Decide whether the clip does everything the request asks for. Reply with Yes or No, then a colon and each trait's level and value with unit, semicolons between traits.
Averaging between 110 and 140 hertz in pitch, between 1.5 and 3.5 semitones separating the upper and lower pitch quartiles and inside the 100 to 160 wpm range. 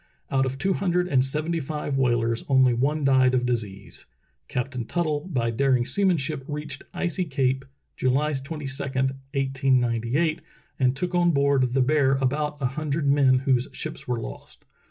Yes: low, 135 Hz; average, 2.9 semitones; average, 155 wpm